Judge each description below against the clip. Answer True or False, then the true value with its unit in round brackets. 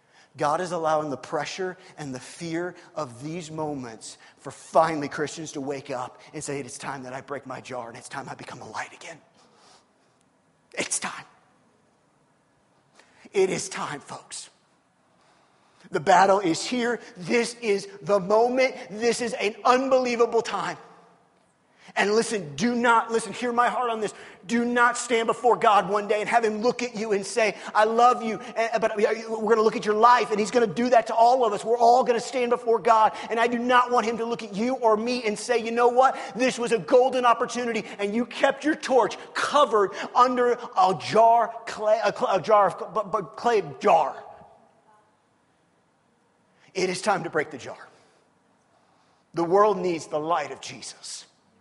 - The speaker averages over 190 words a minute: False (185 wpm)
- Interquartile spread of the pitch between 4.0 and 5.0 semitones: True (4.4 semitones)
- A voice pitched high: True (220 Hz)